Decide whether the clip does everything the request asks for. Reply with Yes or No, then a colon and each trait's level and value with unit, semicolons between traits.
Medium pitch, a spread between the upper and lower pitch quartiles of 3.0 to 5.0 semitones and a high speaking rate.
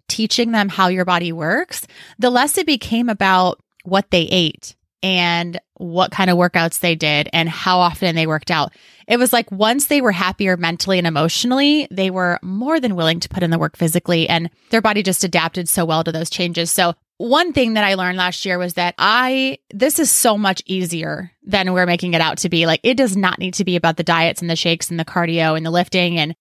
Yes: medium, 180 Hz; average, 3.5 semitones; fast, 230 wpm